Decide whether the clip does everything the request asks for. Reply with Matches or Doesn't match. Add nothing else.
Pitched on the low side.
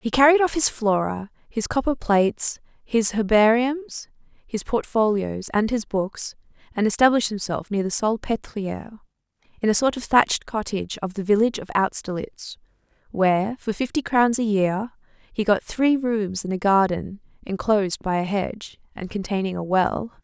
Doesn't match